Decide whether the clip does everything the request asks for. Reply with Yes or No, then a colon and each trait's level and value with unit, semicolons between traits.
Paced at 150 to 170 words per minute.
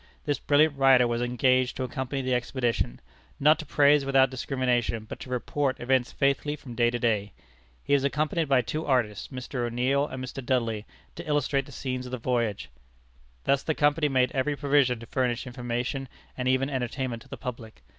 No: average, 185 wpm